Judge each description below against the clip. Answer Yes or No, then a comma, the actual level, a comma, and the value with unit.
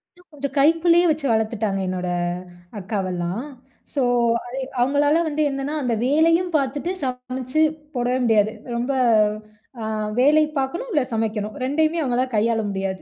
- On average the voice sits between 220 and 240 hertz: No, very high, 255 Hz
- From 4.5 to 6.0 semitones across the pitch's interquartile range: Yes, wide, 5.4 semitones